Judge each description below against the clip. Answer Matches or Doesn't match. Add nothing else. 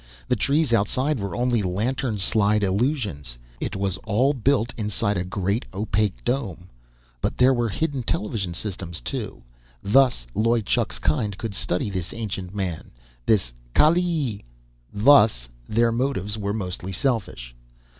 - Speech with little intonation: Doesn't match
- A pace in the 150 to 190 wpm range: Doesn't match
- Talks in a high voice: Doesn't match